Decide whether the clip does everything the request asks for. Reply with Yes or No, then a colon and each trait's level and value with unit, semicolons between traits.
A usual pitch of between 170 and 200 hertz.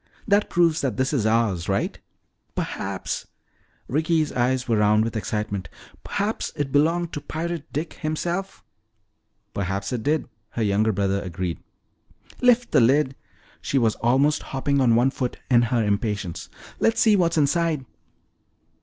No: low, 130 Hz